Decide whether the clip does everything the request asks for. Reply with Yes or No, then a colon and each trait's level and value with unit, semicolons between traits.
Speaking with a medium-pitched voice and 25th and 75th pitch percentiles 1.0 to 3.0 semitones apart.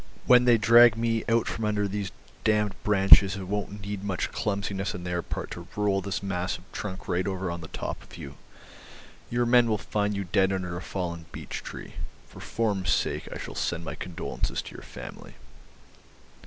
No: low, 100 Hz; narrow, 2.6 semitones